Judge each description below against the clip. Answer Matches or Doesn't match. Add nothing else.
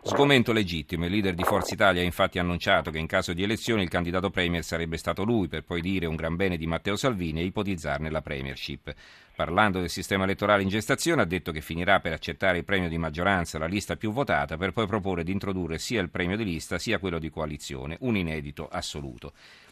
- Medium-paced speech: Doesn't match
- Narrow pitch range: Doesn't match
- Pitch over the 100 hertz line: Doesn't match